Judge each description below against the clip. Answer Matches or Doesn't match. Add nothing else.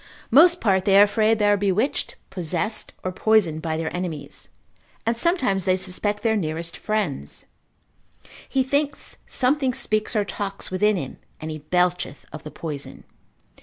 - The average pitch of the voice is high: Matches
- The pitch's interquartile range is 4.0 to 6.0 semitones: Matches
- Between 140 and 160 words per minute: Matches